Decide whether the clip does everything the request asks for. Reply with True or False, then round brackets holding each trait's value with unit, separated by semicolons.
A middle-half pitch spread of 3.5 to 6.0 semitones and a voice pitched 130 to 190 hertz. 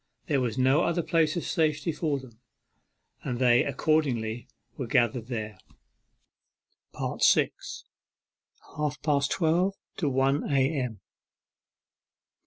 True (4.0 semitones; 135 Hz)